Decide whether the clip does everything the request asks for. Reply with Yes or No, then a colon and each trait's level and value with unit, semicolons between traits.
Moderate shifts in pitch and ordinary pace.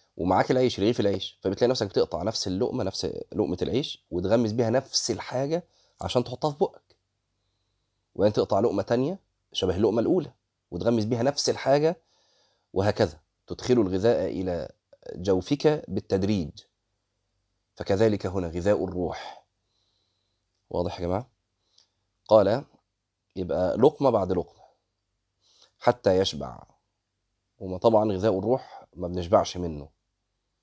Yes: average, 3.3 semitones; average, 115 wpm